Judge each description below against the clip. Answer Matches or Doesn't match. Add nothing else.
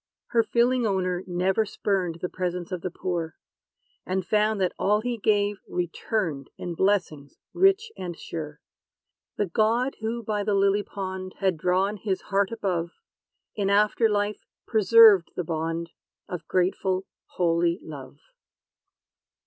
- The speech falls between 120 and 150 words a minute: Matches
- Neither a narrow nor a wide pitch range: Matches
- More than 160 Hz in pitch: Matches